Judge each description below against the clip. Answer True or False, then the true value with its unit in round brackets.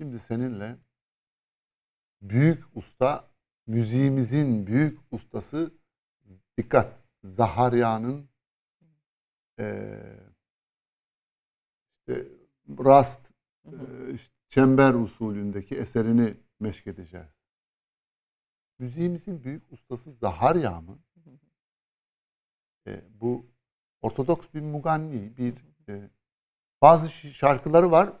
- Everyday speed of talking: False (70 wpm)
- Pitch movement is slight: False (5.4 semitones)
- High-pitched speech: False (125 Hz)